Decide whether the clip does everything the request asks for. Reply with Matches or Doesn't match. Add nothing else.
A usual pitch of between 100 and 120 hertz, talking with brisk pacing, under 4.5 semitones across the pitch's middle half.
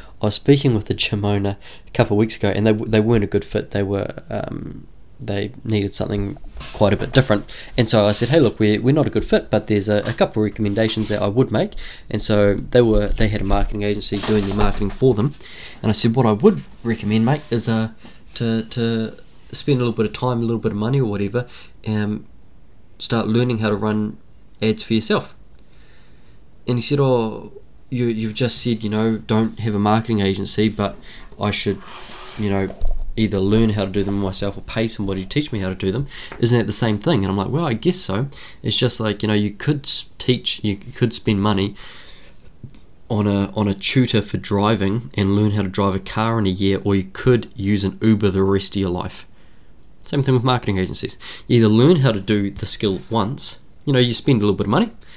Matches